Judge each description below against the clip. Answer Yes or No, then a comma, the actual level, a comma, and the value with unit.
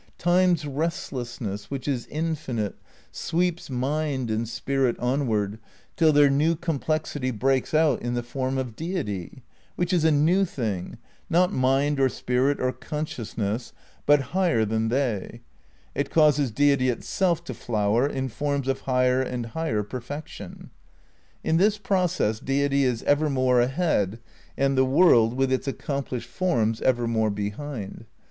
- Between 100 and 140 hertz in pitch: Yes, low, 135 Hz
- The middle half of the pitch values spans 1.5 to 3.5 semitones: No, average, 4.2 semitones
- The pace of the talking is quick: No, average, 140 wpm